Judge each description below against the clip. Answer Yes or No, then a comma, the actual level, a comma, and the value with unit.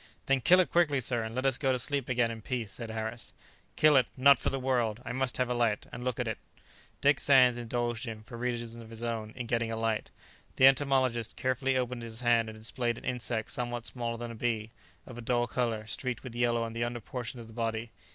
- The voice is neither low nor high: No, low, 120 Hz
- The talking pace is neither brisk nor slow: No, fast, 240 wpm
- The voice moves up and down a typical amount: No, narrow, 2.0 semitones